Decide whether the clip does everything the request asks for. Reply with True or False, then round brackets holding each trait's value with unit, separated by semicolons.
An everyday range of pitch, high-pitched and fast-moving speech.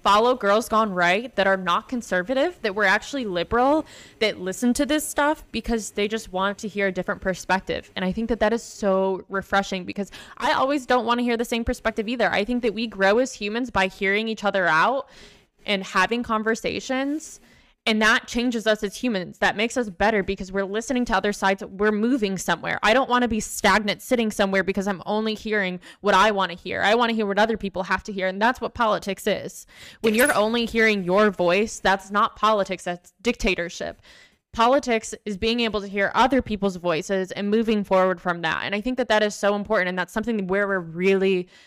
True (3.0 semitones; 210 Hz; 215 wpm)